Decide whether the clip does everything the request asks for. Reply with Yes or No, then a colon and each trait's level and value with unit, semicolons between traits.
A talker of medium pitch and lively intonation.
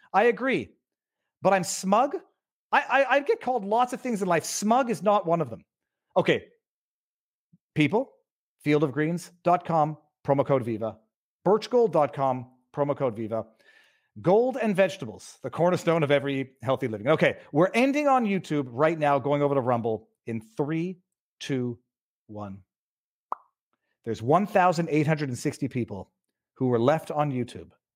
Yes: medium, 150 Hz; wide, 7.1 semitones